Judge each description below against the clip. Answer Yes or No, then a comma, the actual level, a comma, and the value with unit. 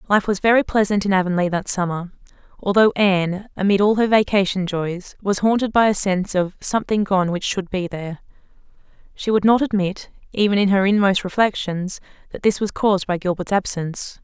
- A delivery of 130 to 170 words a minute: No, average, 180 wpm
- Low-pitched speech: No, high, 195 Hz